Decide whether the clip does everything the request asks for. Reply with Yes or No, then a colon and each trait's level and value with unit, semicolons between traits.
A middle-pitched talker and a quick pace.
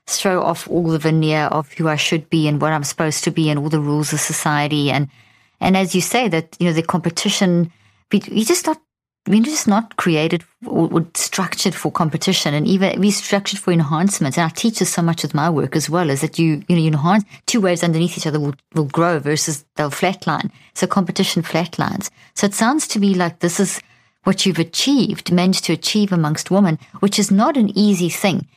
Yes: medium, 175 Hz; fast, 215 wpm